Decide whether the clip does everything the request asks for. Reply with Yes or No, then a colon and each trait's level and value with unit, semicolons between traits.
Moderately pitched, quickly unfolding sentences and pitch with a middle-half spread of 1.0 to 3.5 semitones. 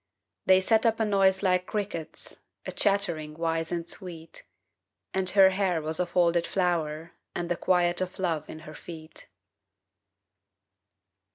No: medium, 175 Hz; average, 145 wpm; average, 2.7 semitones